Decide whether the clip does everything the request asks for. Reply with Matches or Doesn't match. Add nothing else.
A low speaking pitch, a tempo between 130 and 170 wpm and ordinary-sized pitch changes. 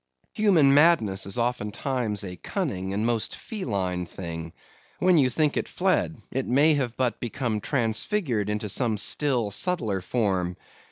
Doesn't match